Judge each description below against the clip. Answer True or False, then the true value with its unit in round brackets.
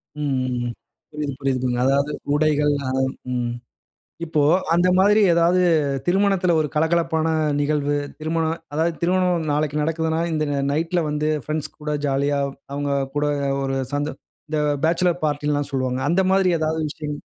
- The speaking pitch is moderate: True (150 Hz)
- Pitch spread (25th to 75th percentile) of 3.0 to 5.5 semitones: False (2.5 semitones)